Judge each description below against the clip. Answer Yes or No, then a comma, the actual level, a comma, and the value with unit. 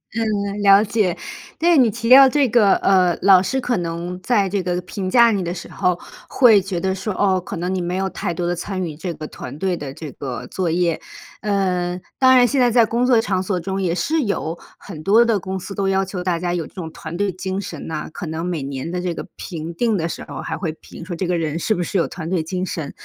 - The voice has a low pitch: No, medium, 185 Hz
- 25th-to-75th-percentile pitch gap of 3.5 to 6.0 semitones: No, average, 3.0 semitones